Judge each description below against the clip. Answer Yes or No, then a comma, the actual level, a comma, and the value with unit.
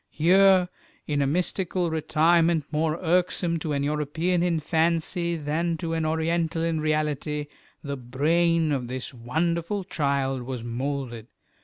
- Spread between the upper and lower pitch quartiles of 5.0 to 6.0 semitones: No, average, 3.0 semitones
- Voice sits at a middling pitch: Yes, medium, 160 Hz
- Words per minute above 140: No, slow, 135 wpm